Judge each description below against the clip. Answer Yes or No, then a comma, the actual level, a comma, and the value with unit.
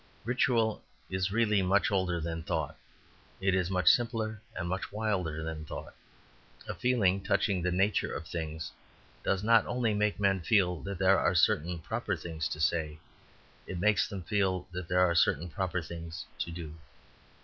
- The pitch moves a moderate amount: Yes, average, 3.5 semitones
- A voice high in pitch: No, very low, 95 Hz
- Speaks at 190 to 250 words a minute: No, average, 170 wpm